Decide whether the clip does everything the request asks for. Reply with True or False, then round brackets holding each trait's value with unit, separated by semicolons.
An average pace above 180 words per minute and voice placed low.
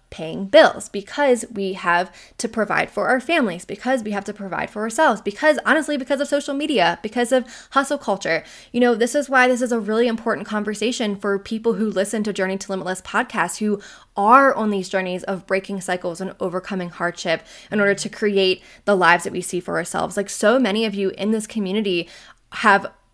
False (200 wpm; 210 Hz)